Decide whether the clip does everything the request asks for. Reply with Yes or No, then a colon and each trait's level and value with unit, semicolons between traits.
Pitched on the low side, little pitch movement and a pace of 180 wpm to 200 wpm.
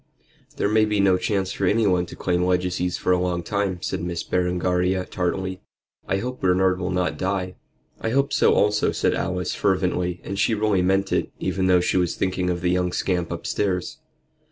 Yes: very low, 90 Hz; narrow, 1.5 semitones; average, 190 wpm